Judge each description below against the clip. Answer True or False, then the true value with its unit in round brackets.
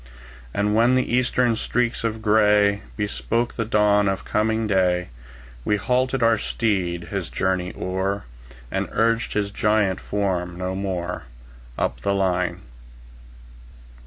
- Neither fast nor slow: False (130 wpm)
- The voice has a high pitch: False (105 Hz)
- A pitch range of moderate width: True (3.1 semitones)